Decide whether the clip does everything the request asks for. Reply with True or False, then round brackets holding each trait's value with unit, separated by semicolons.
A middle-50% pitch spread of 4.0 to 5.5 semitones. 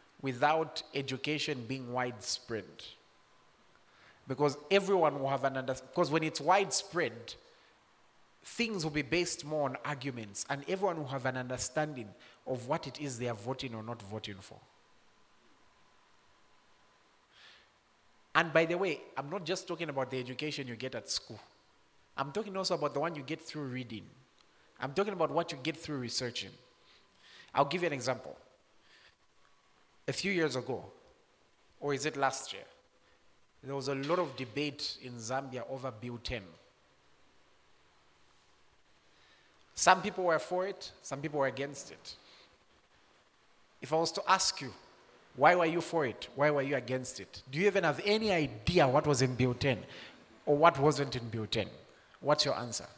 True (4.3 semitones)